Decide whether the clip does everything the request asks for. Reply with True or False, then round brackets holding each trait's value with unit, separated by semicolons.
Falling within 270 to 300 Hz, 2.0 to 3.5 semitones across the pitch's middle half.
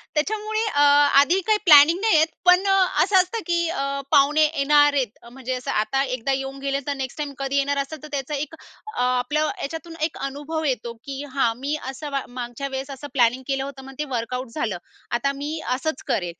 True (280 Hz; 2.9 semitones)